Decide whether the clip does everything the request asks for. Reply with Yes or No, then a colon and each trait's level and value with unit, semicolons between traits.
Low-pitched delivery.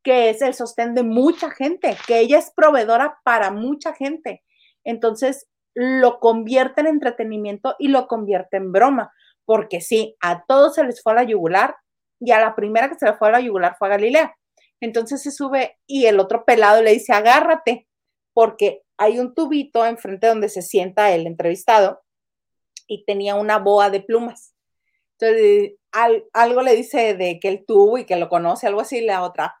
No: high, 230 Hz